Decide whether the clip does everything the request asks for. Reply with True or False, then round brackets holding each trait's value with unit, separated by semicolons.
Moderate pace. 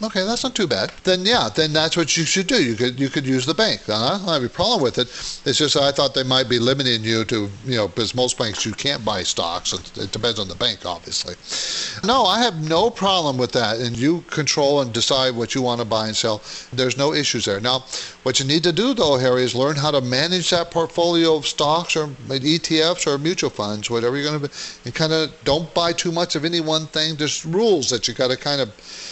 False (250 wpm)